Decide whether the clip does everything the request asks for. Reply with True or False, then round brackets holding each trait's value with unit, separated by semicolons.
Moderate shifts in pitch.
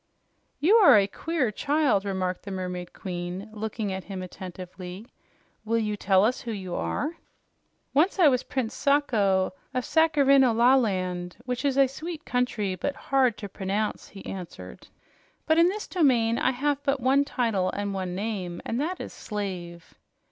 False (6.5 semitones)